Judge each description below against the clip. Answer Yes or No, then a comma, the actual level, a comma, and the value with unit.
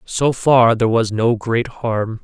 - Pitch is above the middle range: No, low, 115 Hz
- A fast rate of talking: No, average, 190 wpm